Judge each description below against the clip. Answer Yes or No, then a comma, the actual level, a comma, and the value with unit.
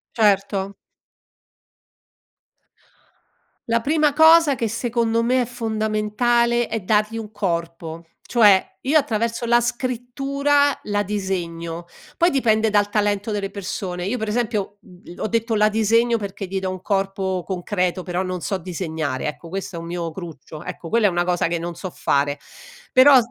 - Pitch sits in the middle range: No, high, 205 Hz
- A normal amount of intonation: Yes, average, 4.3 semitones